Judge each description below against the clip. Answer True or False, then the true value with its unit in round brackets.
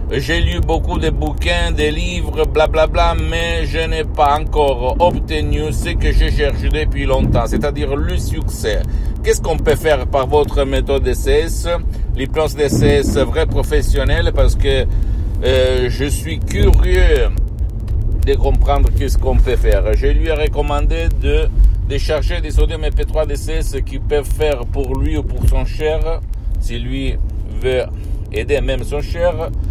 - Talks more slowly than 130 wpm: False (155 wpm)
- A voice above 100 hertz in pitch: False (90 Hz)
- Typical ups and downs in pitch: False (6.6 semitones)